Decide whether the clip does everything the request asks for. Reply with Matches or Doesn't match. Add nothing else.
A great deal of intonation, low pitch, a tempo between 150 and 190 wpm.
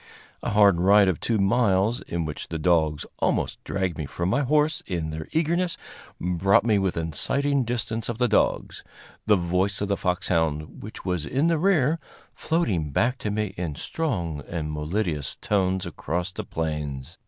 Matches